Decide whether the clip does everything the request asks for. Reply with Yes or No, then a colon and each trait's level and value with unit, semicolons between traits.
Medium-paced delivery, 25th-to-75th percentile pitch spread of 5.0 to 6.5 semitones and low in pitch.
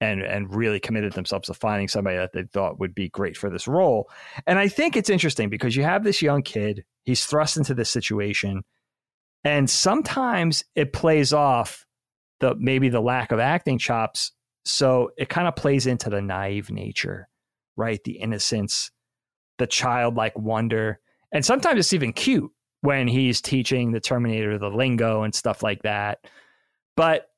Yes: average, 170 wpm; wide, 5.5 semitones; low, 120 Hz